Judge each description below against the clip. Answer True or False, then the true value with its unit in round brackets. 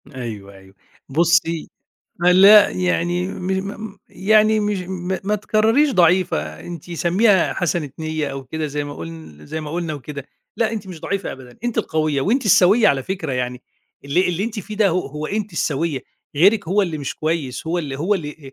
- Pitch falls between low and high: True (170 Hz)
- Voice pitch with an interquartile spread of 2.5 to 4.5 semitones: False (5.3 semitones)